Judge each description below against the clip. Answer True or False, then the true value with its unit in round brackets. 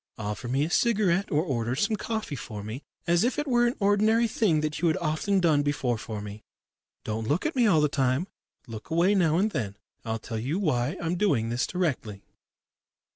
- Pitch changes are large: True (8.8 semitones)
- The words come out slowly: False (205 wpm)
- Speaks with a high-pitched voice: False (155 Hz)